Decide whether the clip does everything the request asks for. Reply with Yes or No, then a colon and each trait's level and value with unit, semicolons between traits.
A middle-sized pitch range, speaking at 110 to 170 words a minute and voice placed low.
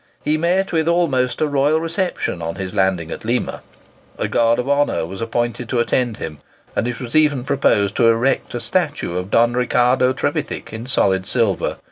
No: average, 4.7 semitones; average, 185 wpm; low, 125 Hz